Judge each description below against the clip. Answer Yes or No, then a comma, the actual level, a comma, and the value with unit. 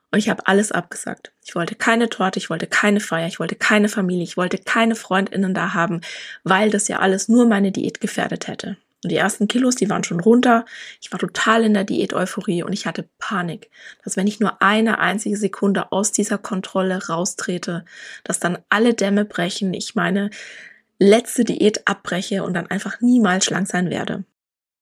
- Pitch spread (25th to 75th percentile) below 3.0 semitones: Yes, narrow, 2.5 semitones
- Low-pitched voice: No, high, 200 Hz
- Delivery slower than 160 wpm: No, fast, 190 wpm